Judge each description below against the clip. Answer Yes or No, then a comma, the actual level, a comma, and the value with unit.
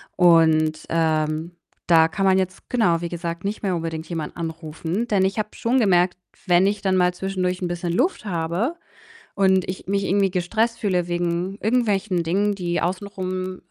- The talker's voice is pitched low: No, medium, 180 Hz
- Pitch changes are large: No, average, 2.7 semitones